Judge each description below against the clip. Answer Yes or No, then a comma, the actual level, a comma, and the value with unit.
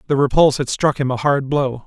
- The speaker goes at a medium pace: No, fast, 255 wpm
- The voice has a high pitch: No, medium, 140 Hz